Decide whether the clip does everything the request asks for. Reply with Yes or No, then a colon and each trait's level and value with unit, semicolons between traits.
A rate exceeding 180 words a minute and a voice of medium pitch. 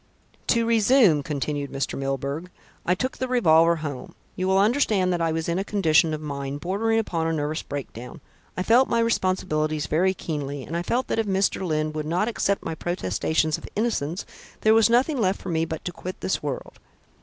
Yes: average, 200 wpm; medium, 170 Hz